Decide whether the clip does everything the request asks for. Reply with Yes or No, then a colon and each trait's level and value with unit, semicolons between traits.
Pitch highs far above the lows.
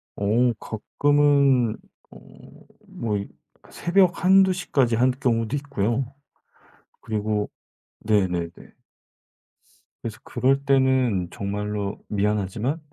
No: average, 4.9 semitones